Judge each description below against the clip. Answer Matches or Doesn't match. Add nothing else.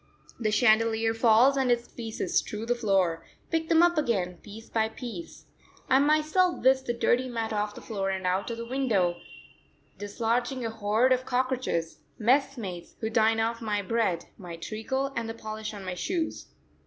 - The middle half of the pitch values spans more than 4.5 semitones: Doesn't match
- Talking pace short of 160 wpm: Doesn't match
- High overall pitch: Matches